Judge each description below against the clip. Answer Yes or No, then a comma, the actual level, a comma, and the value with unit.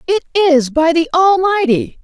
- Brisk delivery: No, average, 145 wpm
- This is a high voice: Yes, very high, 335 Hz